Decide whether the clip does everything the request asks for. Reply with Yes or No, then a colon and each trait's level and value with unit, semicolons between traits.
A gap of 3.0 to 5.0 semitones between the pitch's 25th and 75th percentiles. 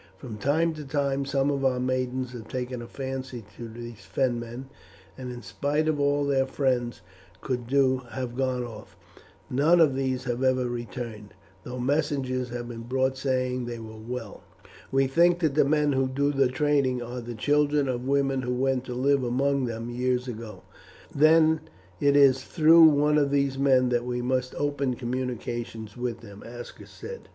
No: narrow, 2.4 semitones